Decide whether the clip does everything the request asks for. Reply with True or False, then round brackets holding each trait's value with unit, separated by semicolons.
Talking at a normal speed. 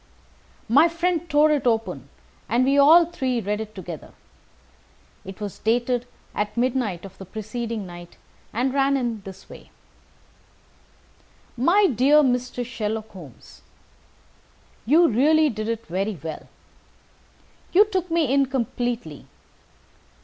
False (125 wpm)